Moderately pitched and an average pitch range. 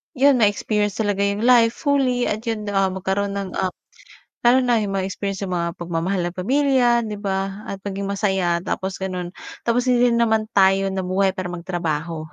No: high, 200 Hz; average, 3.5 semitones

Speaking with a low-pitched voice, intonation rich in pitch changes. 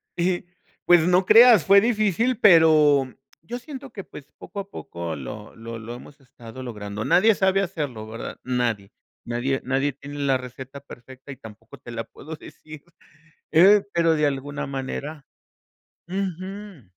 No: medium, 145 Hz; wide, 7.1 semitones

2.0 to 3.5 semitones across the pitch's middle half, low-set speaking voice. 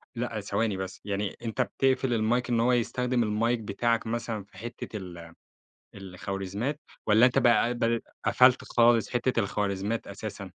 Yes: average, 2.9 semitones; low, 115 Hz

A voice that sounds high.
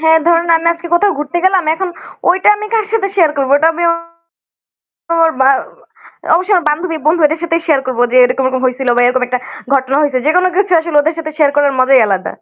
Yes: very high, 315 Hz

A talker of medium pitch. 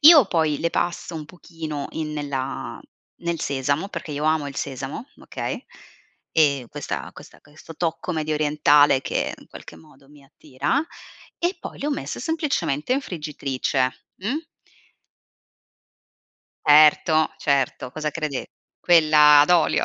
Yes: medium, 150 Hz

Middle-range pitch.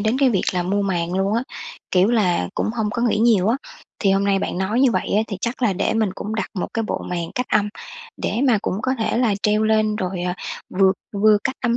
No: high, 210 Hz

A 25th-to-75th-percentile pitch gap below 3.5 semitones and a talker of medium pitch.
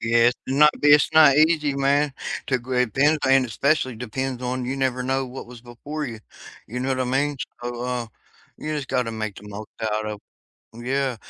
No: narrow, 2.6 semitones; low, 130 Hz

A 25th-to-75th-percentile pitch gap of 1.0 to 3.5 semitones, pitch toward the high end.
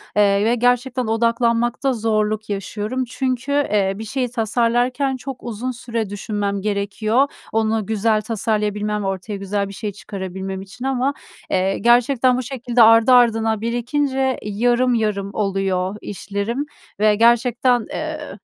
Yes: average, 3.2 semitones; high, 225 Hz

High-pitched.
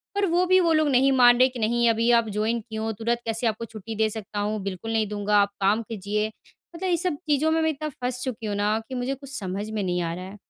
Yes: high, 225 Hz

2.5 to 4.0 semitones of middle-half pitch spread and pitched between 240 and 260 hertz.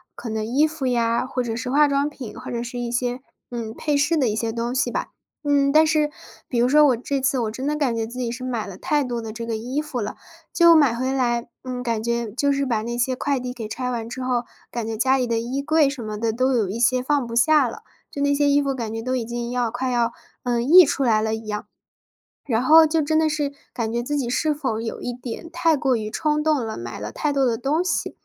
Yes: average, 3.5 semitones; very high, 250 Hz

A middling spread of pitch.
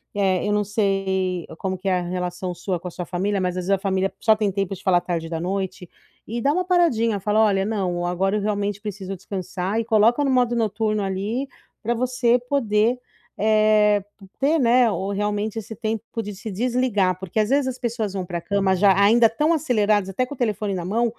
Yes: average, 3.2 semitones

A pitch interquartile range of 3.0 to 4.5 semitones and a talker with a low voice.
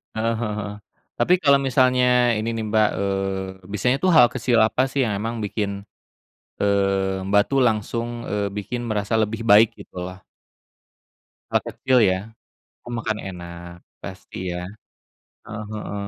Yes: average, 3.4 semitones; low, 105 Hz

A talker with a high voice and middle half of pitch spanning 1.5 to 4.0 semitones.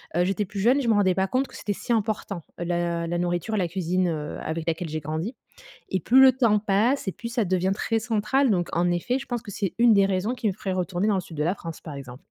No: high, 195 Hz; average, 4.4 semitones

